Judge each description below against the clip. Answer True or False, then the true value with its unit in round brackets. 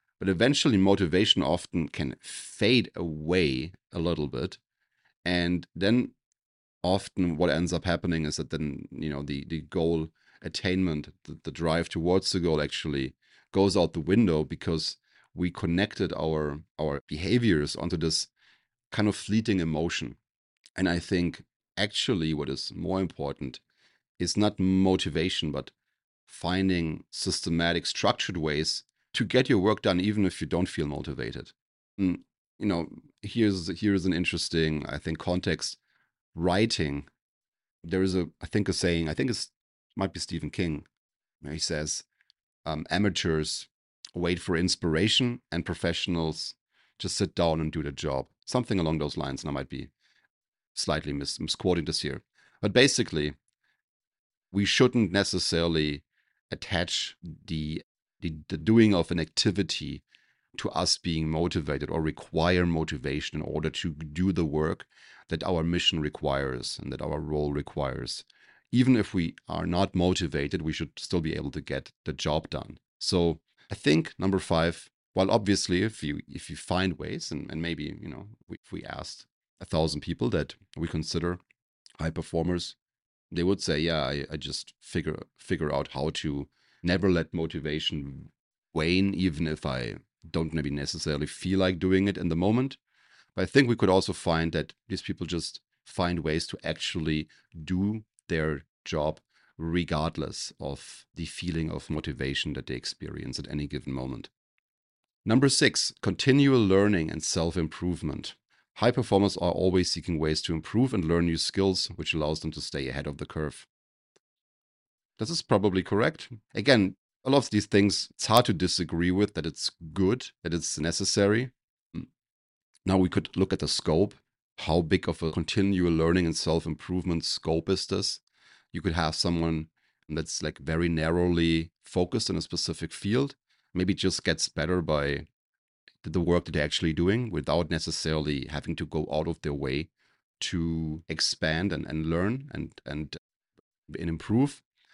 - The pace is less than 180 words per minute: True (155 wpm)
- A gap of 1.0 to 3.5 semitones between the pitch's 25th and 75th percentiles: True (3.2 semitones)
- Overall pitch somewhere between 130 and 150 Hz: False (85 Hz)